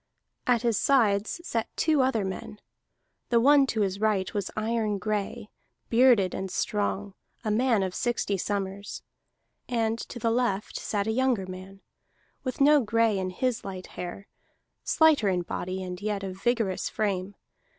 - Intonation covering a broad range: No, average, 3.6 semitones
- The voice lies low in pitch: No, high, 210 Hz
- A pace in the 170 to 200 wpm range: No, average, 155 wpm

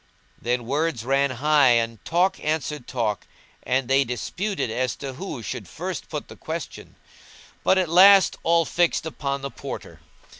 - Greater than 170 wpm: No, average, 155 wpm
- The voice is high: No, medium, 140 Hz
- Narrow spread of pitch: No, average, 5.2 semitones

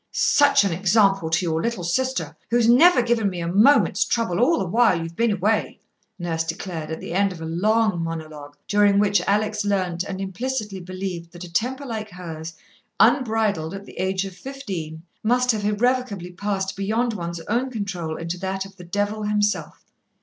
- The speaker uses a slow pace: No, average, 180 wpm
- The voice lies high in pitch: Yes, high, 195 Hz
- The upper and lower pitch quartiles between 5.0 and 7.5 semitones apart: No, average, 4.3 semitones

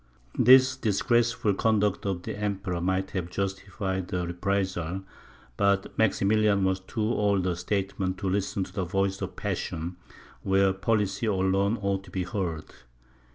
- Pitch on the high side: No, very low, 95 Hz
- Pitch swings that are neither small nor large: No, narrow, 1.7 semitones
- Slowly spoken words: No, average, 145 wpm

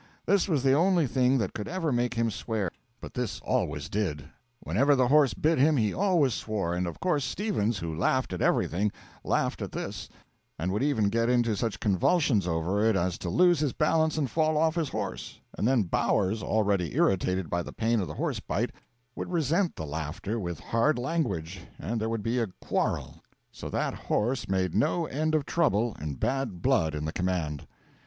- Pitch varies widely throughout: Yes, wide, 7.7 semitones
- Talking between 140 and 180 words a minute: No, average, 195 wpm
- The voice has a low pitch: Yes, low, 115 Hz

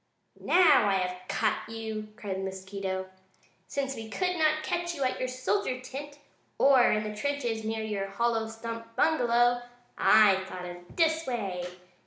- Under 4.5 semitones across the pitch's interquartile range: No, wide, 5.5 semitones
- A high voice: Yes, high, 225 Hz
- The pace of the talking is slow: No, average, 160 wpm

